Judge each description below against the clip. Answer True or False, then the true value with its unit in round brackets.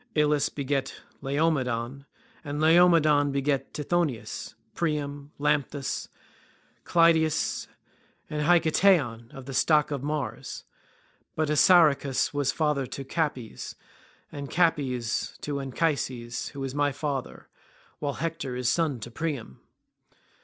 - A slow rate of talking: True (110 wpm)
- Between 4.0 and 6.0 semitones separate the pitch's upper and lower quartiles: False (2.7 semitones)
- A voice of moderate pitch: True (145 Hz)